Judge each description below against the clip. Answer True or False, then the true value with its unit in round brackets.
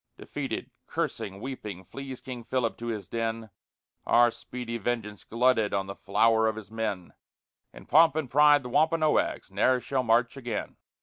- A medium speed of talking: True (160 wpm)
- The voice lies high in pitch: False (115 Hz)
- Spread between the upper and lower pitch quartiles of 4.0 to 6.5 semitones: False (2.9 semitones)